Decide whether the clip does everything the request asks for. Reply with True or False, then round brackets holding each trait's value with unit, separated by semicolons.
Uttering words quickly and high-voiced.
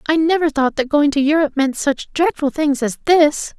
True (215 wpm; 295 Hz)